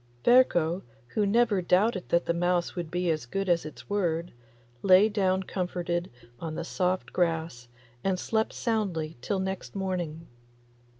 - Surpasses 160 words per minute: No, average, 145 wpm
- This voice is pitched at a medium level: Yes, medium, 180 Hz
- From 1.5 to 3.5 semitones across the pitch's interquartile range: Yes, narrow, 2.6 semitones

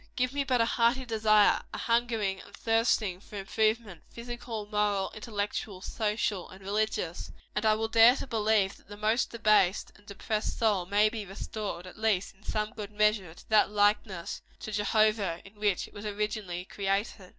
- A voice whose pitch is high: Yes, high, 210 Hz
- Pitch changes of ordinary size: No, narrow, 1.9 semitones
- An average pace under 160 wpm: No, average, 175 wpm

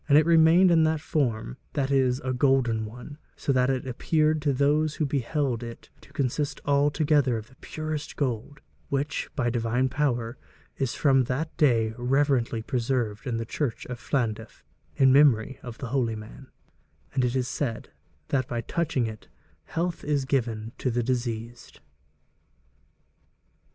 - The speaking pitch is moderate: No, low, 130 Hz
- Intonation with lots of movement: No, average, 3.6 semitones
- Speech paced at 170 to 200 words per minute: No, average, 155 wpm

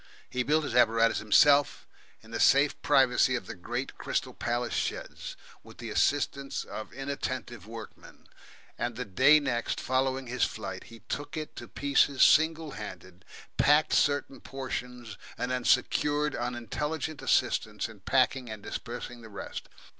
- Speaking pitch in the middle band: No, low, 125 Hz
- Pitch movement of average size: Yes, average, 3.4 semitones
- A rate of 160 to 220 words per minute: No, average, 145 wpm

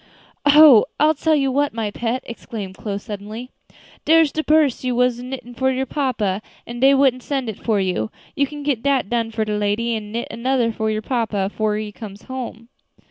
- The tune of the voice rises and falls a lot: No, average, 3.8 semitones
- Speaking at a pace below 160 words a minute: No, average, 200 wpm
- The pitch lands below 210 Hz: No, high, 235 Hz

